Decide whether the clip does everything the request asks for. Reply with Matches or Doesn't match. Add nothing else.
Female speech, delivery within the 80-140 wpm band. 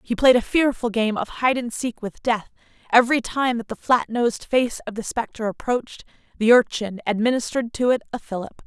Doesn't match